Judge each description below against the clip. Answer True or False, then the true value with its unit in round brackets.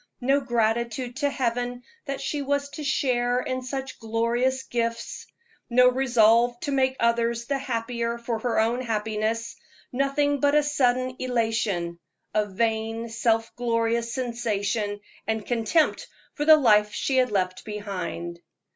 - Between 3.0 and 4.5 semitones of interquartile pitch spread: False (2.6 semitones)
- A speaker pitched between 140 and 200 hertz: False (235 Hz)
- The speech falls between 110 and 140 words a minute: True (135 wpm)